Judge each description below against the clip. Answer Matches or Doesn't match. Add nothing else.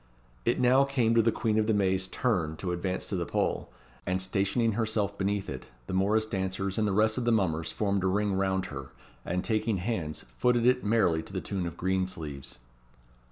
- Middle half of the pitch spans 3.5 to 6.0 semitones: Doesn't match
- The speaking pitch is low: Matches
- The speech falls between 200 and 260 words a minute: Matches